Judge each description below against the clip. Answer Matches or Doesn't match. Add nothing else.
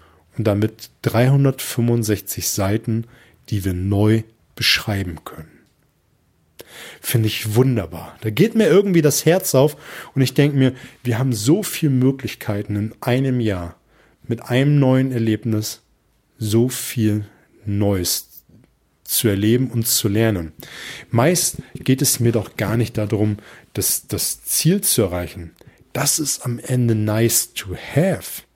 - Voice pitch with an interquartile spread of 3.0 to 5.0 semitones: Matches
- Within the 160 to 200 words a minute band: Doesn't match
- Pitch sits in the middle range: Doesn't match